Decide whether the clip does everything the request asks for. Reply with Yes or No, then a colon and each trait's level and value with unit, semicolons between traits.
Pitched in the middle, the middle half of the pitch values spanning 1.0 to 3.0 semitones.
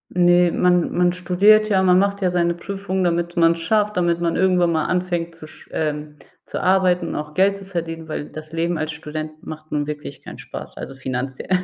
Yes: medium, 170 Hz; average, 2.7 semitones